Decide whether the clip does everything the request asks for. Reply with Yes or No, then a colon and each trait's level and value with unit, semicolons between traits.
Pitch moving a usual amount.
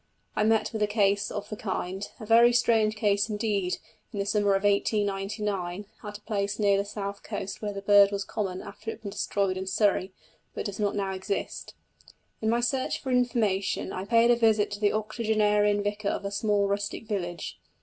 No: narrow, 1.4 semitones